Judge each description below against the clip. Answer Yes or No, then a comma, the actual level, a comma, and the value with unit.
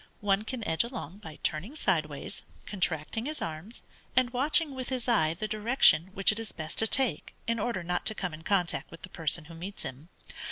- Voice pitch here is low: No, high, 195 Hz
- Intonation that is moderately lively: No, wide, 6.3 semitones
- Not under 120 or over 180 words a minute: No, fast, 205 wpm